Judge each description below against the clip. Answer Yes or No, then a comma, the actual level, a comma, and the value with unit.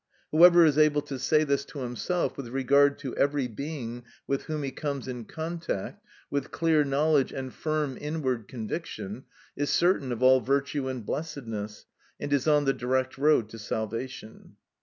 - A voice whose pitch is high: No, medium, 140 Hz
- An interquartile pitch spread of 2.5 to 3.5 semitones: Yes, average, 3.1 semitones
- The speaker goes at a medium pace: Yes, average, 165 wpm